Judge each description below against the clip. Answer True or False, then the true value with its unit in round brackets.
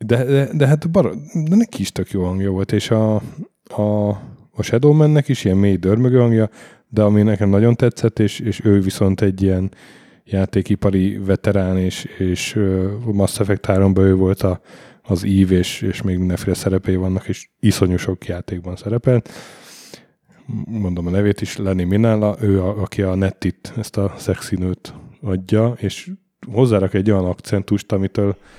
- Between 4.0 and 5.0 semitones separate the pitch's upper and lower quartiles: False (2.9 semitones)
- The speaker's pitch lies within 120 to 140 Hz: False (100 Hz)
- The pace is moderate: False (160 wpm)